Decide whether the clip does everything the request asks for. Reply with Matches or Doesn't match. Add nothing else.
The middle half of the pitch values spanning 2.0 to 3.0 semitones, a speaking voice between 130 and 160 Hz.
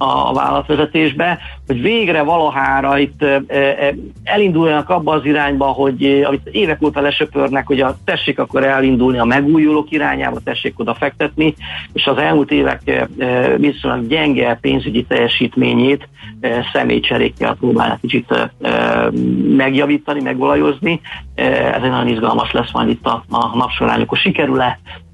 Matches